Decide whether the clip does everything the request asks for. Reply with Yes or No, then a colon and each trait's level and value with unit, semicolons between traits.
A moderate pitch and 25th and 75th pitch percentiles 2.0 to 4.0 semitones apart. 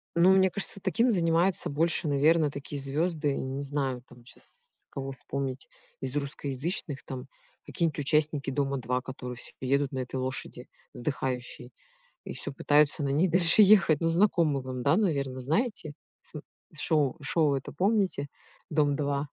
Yes: medium, 145 Hz; average, 3.6 semitones